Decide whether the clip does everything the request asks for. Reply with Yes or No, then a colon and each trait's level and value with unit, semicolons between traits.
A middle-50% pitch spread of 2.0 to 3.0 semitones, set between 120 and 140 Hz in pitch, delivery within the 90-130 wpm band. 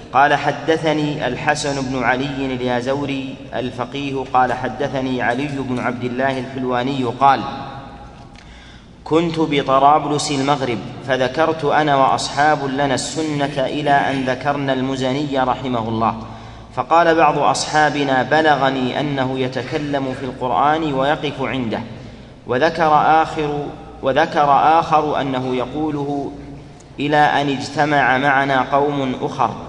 Yes: narrow, 2.4 semitones; low, 135 Hz; average, 105 wpm